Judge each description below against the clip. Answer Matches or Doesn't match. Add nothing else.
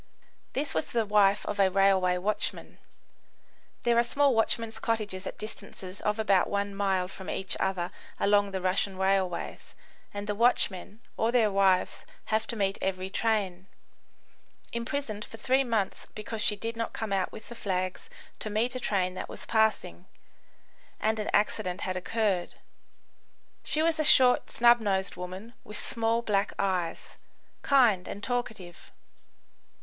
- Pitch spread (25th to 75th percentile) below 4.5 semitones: Matches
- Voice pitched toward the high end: Matches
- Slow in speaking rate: Doesn't match